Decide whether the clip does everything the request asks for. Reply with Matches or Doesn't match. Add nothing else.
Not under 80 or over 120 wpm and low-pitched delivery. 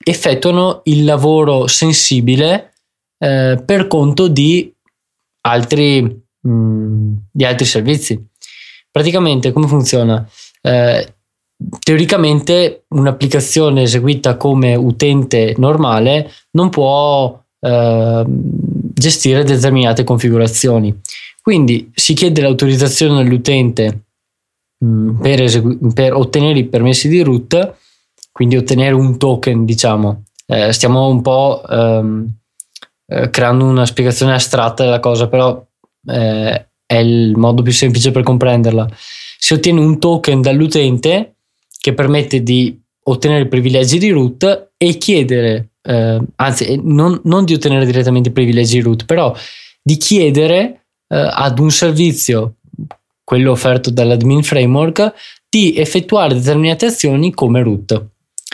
Matches